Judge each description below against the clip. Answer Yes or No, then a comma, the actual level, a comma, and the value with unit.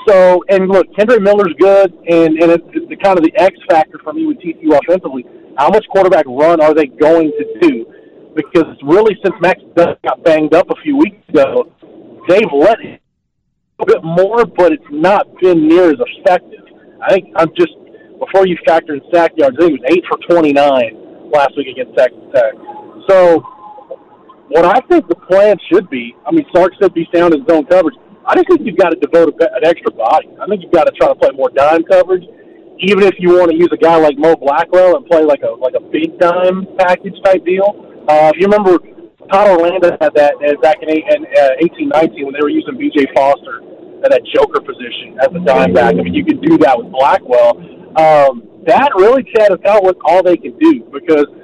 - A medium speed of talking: No, fast, 210 wpm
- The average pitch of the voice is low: No, medium, 185 Hz